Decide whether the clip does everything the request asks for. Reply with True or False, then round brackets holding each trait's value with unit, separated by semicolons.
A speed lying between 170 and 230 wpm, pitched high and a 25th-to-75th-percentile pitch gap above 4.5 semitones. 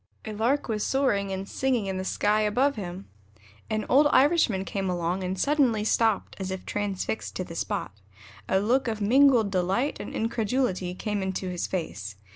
False (175 wpm; 210 Hz; 4.2 semitones)